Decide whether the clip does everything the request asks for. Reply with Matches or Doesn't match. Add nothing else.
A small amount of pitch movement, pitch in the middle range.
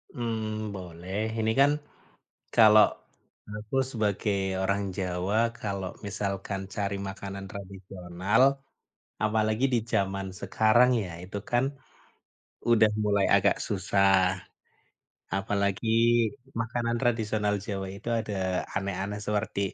Doesn't match